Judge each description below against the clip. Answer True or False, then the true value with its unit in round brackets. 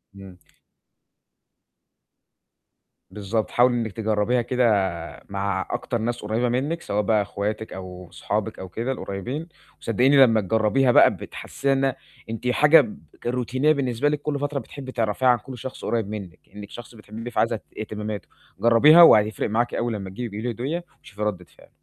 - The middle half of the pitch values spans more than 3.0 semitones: True (3.6 semitones)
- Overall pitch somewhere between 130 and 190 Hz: False (115 Hz)